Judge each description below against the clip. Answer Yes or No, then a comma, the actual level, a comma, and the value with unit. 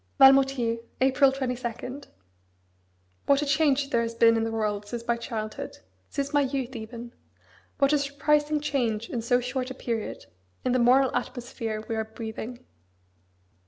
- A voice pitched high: Yes, very high, 250 Hz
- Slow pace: No, average, 155 wpm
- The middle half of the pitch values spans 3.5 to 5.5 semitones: No, average, 3.0 semitones